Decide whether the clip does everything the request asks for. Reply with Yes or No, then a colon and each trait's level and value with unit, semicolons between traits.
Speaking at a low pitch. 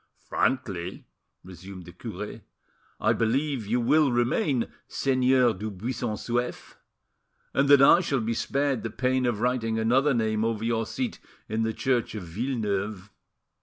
Yes: low, 115 Hz